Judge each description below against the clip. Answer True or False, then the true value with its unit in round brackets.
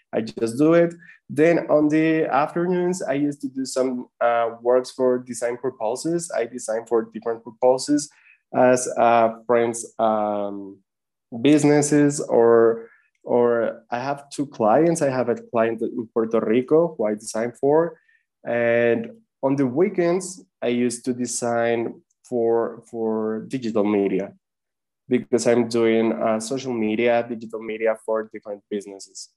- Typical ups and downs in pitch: True (4.0 semitones)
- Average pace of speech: True (140 wpm)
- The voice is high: False (120 Hz)